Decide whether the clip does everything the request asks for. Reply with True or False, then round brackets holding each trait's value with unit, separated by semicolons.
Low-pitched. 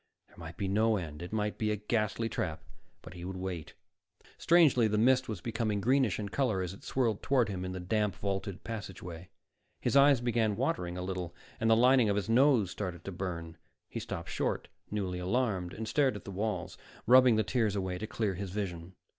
True (105 Hz)